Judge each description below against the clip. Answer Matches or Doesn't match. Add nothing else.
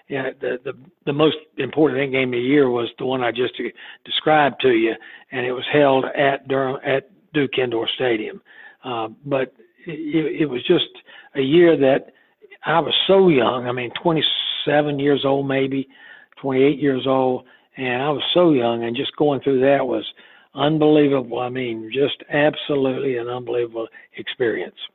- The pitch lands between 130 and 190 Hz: Matches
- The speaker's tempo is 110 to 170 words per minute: Matches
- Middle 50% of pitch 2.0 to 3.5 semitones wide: Matches